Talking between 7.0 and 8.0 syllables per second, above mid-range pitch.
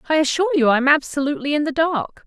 Yes: 7.4 syllables/s; very high, 290 Hz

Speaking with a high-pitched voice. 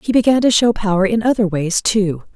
Yes: high, 205 Hz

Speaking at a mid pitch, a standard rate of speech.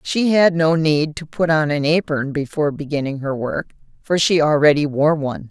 Yes: medium, 150 Hz; average, 195 wpm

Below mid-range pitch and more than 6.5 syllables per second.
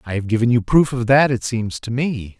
No: low, 120 Hz; 5.2 syllables/s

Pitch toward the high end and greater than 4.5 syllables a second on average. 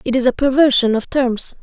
Yes: very high, 255 Hz; 5.4 syllables/s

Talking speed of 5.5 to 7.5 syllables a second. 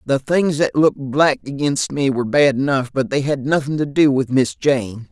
No: 4.9 syllables/s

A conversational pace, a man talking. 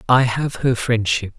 Yes: average, 175 wpm; male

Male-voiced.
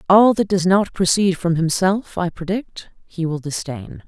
No: female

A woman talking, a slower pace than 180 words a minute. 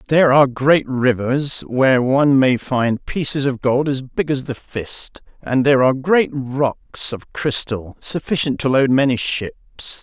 No: male; average, 170 wpm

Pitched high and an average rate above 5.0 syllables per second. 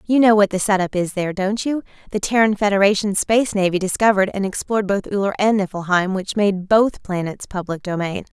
Yes: high, 200 Hz; 5.8 syllables/s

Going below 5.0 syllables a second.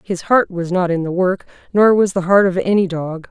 No: 5.1 syllables/s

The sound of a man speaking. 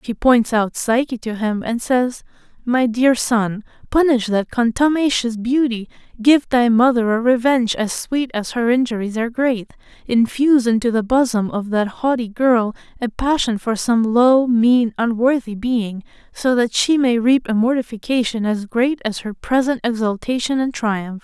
No: female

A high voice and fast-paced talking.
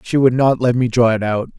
No: low, 120 Hz; fast, 300 wpm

